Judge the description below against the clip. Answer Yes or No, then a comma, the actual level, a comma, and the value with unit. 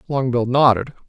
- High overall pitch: No, low, 125 Hz